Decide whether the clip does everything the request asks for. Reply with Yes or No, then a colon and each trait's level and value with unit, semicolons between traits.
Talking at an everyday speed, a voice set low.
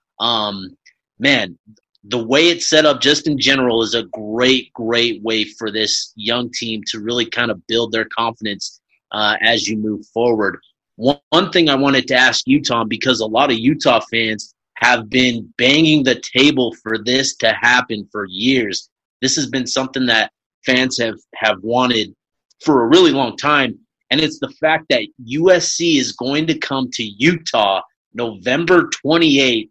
Yes: average, 170 wpm; low, 125 Hz